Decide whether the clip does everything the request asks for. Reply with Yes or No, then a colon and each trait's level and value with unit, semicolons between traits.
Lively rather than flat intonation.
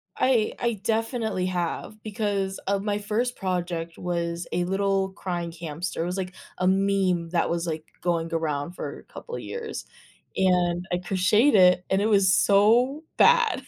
No: average, 3.2 semitones